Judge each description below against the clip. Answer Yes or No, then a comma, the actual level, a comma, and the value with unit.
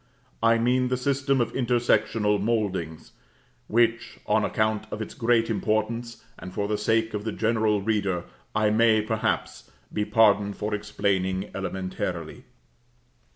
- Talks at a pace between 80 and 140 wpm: Yes, slow, 135 wpm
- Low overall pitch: Yes, low, 110 Hz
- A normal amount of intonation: No, narrow, 2.0 semitones